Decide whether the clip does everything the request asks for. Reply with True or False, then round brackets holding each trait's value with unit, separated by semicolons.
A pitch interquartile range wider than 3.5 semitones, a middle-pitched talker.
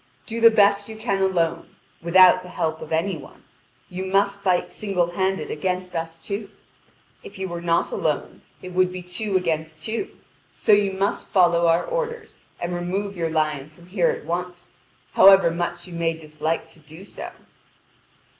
False (3.0 semitones; 180 Hz)